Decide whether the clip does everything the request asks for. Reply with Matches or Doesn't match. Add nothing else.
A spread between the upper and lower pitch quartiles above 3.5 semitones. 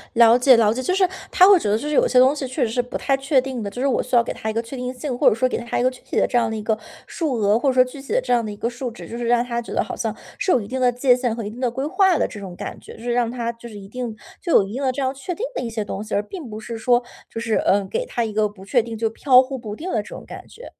Doesn't match